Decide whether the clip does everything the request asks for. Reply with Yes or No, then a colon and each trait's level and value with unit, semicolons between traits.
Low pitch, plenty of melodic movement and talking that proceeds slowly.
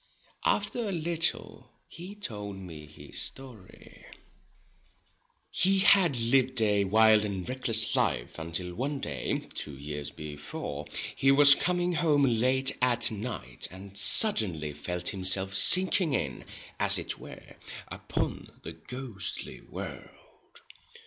Yes: low, 110 Hz; wide, 7.8 semitones; slow, 120 wpm